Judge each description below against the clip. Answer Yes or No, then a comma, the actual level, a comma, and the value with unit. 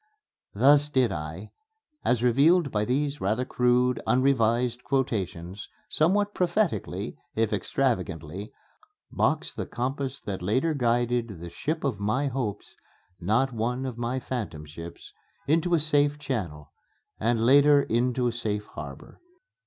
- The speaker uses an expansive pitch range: No, average, 4.8 semitones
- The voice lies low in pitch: Yes, low, 125 Hz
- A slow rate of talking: Yes, slow, 130 wpm